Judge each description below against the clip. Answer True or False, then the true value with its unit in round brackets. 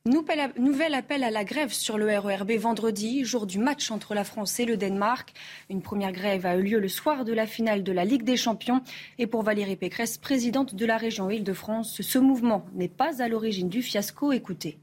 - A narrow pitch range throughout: False (3.8 semitones)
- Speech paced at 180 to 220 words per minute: True (210 wpm)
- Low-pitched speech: False (225 Hz)